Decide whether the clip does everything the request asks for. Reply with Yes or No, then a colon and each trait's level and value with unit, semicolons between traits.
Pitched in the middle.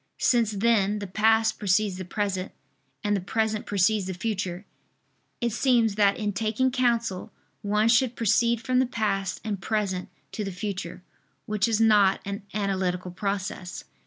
No: high, 210 Hz